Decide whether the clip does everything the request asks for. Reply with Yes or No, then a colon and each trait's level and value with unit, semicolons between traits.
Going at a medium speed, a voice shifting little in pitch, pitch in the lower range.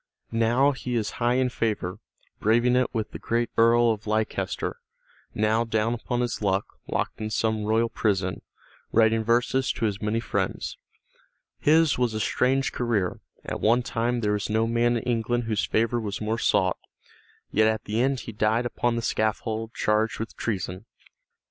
Yes: average, 170 wpm; narrow, 1.8 semitones; low, 115 Hz